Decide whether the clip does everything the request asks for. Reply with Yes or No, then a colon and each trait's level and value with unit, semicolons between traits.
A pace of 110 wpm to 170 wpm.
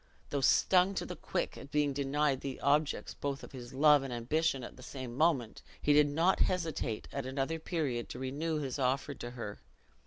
No: average, 195 wpm